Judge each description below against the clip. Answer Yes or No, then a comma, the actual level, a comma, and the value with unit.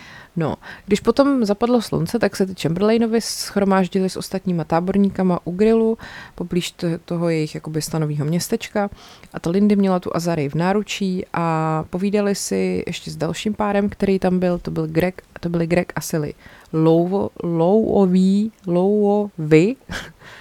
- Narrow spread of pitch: No, average, 3.6 semitones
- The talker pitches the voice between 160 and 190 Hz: Yes, medium, 185 Hz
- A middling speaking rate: Yes, average, 145 wpm